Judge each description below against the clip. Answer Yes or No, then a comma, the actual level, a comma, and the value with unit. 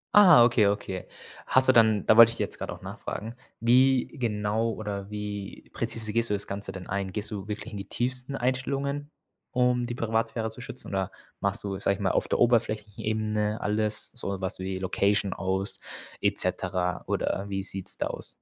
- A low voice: Yes, low, 105 Hz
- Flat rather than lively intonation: No, average, 3.1 semitones